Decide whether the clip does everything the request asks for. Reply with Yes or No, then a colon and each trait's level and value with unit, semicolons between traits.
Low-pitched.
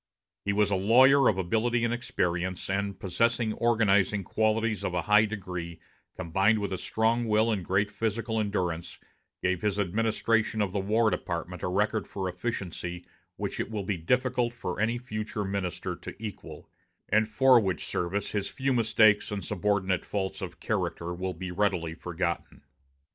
Yes: low, 105 Hz